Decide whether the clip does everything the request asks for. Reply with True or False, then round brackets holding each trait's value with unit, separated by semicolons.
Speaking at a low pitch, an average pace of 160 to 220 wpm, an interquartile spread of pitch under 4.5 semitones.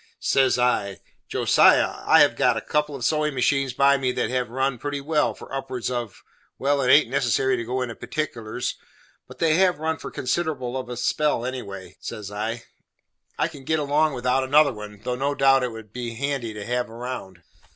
True (130 Hz; 195 wpm; 3.1 semitones)